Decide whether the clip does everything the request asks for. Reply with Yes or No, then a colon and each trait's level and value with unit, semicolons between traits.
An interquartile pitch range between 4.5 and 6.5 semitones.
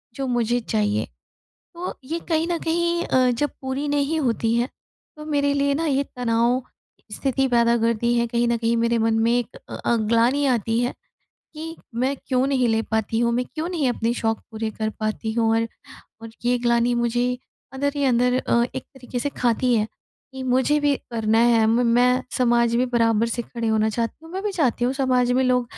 No: average, 2.9 semitones